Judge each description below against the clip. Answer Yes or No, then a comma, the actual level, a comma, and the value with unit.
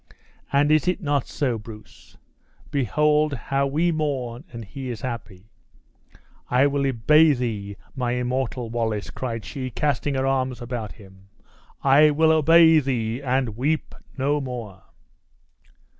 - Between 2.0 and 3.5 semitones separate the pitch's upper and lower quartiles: No, average, 3.9 semitones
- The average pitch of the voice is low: Yes, low, 130 Hz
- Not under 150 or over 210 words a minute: No, slow, 135 wpm